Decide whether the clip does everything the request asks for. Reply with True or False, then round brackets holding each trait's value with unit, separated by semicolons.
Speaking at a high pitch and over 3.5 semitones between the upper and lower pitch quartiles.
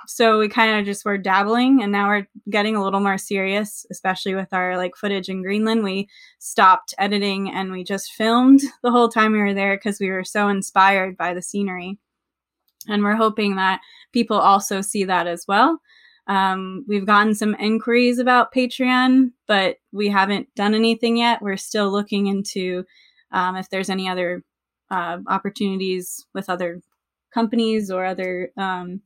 False (200 Hz; 2.5 semitones)